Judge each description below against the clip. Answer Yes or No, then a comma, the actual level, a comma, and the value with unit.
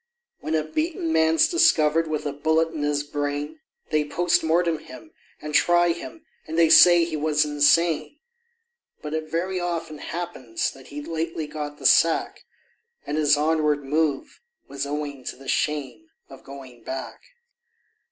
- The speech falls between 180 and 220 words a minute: No, average, 155 wpm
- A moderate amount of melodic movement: No, narrow, 2.2 semitones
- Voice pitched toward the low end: No, medium, 155 Hz